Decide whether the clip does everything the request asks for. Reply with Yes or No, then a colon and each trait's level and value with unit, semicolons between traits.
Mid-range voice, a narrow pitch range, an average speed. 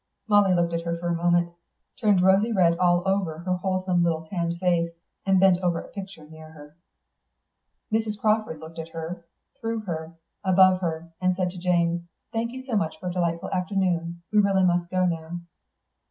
Yes: medium, 175 Hz; narrow, 2.3 semitones; average, 190 wpm